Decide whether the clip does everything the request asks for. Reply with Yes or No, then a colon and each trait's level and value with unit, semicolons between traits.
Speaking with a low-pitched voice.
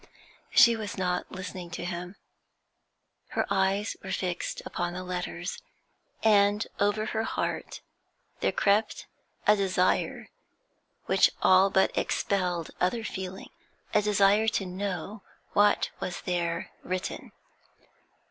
No: high, 190 Hz